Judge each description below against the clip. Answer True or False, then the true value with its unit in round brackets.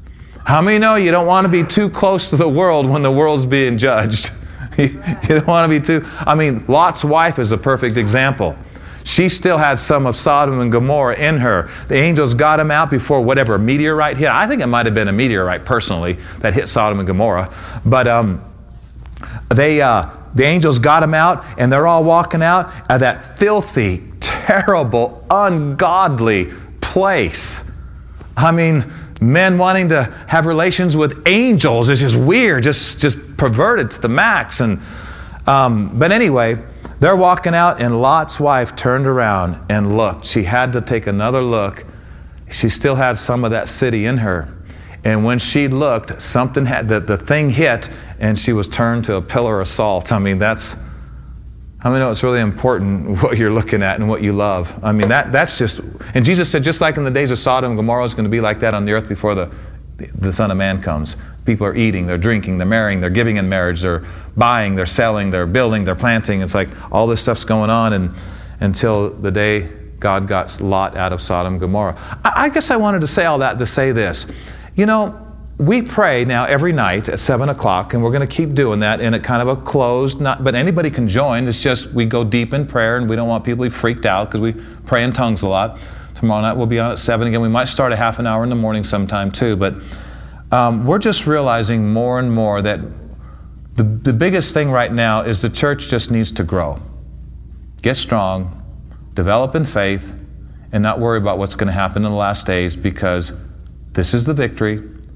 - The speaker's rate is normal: False (210 wpm)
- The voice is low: True (115 Hz)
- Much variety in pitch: True (5.8 semitones)